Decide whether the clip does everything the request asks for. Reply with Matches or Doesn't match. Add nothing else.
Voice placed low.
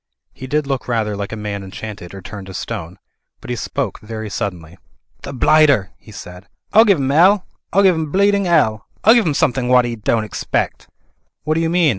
Matches